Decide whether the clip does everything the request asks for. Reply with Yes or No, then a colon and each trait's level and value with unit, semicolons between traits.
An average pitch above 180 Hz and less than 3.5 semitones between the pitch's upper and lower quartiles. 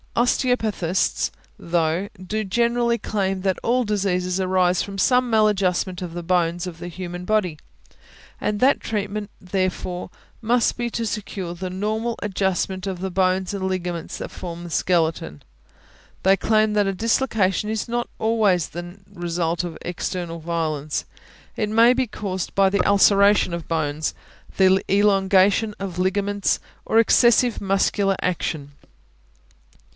Yes: high, 190 Hz; average, 3.0 semitones